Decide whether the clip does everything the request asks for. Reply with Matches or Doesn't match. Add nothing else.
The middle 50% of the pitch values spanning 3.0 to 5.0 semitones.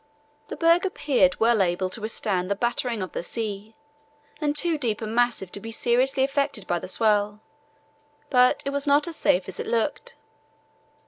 Doesn't match